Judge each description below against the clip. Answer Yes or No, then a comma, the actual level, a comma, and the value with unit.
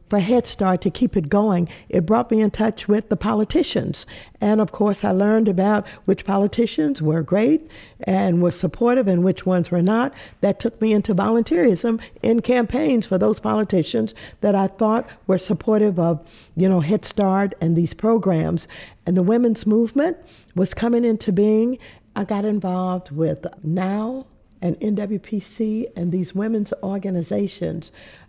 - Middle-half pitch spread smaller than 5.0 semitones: Yes, average, 3.2 semitones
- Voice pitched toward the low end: No, high, 205 Hz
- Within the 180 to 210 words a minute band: No, average, 160 wpm